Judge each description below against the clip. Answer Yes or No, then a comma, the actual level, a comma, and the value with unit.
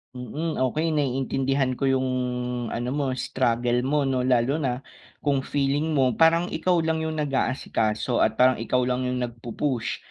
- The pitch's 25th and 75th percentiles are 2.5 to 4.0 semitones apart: Yes, average, 2.9 semitones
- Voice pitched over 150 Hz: No, low, 130 Hz